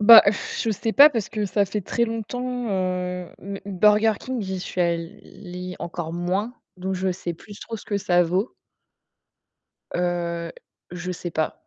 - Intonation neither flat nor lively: Yes, average, 3.3 semitones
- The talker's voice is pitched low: No, high, 190 Hz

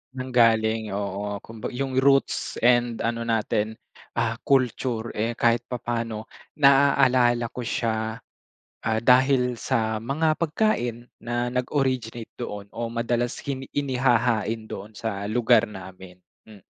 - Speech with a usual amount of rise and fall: No, narrow, 2.3 semitones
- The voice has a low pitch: Yes, low, 115 Hz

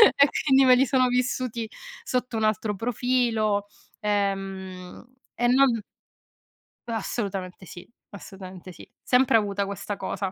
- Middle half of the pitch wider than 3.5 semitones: Yes, average, 4.2 semitones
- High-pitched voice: Yes, high, 215 Hz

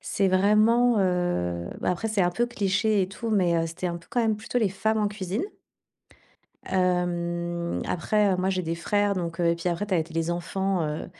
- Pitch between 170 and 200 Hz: Yes, medium, 185 Hz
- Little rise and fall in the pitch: No, average, 3.3 semitones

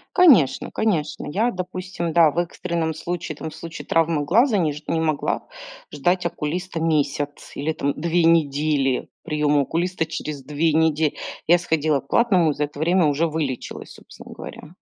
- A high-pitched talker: No, medium, 160 Hz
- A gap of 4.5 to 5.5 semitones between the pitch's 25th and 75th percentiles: No, average, 2.7 semitones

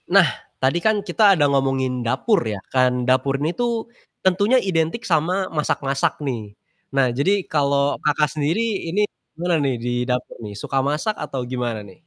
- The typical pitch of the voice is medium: Yes, medium, 145 Hz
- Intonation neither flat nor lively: No, wide, 6.5 semitones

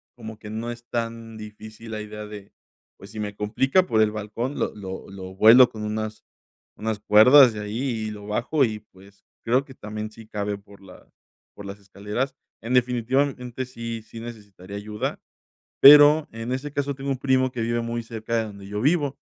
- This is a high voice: No, low, 110 Hz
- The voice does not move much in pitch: No, average, 3.0 semitones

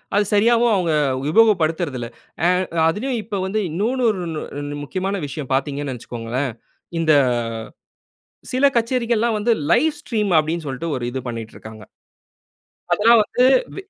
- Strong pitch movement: Yes, wide, 8.1 semitones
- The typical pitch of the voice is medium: Yes, medium, 180 Hz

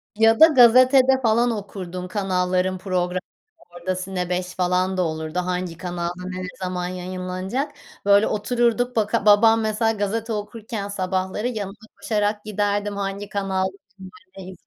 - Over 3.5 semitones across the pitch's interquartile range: No, average, 3.2 semitones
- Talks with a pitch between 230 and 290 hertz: No, high, 200 Hz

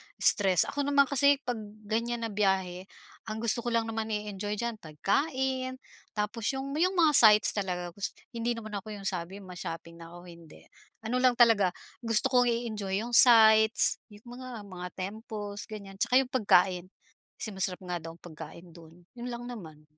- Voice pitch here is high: Yes, high, 210 Hz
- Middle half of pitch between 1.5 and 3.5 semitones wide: No, average, 4.4 semitones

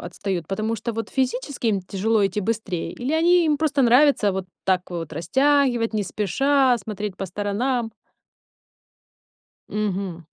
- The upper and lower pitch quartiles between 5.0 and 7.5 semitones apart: Yes, average, 5.3 semitones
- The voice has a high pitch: Yes, high, 215 Hz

